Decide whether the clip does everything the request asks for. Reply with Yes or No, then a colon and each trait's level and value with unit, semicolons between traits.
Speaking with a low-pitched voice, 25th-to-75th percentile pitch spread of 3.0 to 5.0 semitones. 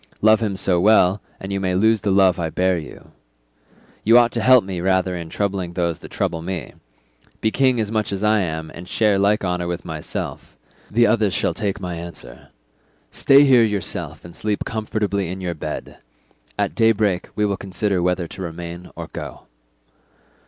Yes: very low, 95 Hz; average, 3.4 semitones